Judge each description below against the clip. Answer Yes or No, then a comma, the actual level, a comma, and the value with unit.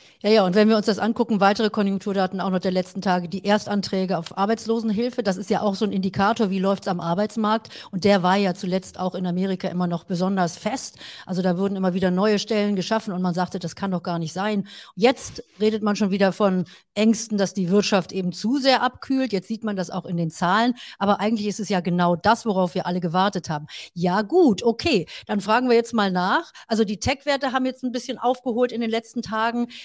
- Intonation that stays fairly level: No, average, 3.2 semitones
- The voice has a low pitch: No, high, 205 Hz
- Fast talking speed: Yes, fast, 230 wpm